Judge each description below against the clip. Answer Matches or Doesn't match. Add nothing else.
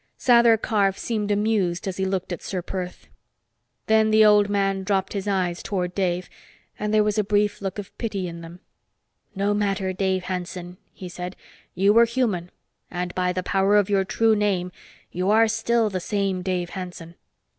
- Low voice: Doesn't match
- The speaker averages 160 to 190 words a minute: Matches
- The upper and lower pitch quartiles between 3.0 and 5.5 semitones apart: Doesn't match